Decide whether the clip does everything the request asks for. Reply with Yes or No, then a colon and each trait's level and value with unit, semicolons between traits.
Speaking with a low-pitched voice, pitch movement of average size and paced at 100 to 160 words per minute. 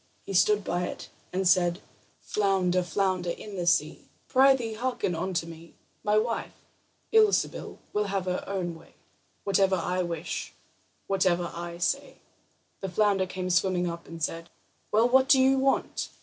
No: medium, 185 Hz; average, 3.4 semitones; average, 150 wpm